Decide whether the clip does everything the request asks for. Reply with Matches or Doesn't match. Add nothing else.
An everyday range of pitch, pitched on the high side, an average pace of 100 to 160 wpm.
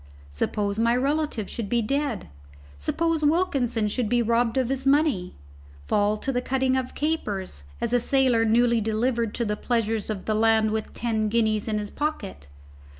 Doesn't match